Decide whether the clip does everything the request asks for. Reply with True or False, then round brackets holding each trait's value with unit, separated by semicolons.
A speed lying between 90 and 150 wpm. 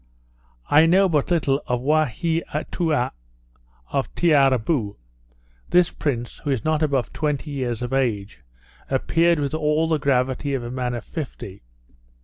True (135 wpm)